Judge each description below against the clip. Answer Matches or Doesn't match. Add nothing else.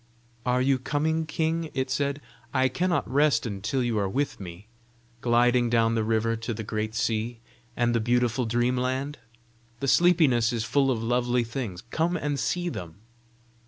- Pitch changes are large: Doesn't match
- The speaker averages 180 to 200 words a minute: Doesn't match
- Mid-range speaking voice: Doesn't match